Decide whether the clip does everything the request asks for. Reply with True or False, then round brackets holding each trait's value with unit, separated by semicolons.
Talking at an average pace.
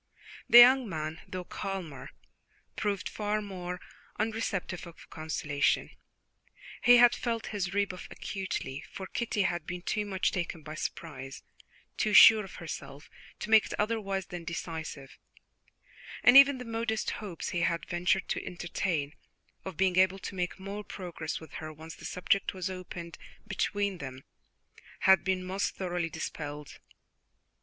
True (145 wpm)